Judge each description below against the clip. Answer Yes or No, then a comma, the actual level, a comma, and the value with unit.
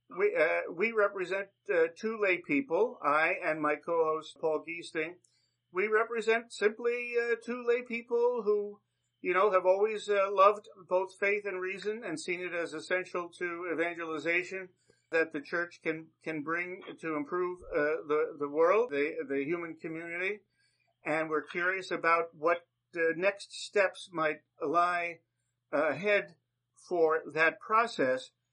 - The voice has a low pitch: No, medium, 180 Hz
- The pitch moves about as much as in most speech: Yes, average, 4.3 semitones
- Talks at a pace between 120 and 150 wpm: Yes, average, 145 wpm